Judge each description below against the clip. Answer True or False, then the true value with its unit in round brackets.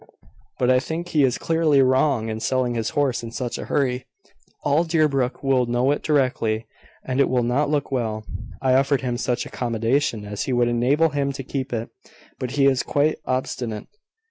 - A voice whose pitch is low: True (130 Hz)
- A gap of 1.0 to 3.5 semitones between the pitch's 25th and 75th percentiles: True (2.8 semitones)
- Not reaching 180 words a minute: False (185 wpm)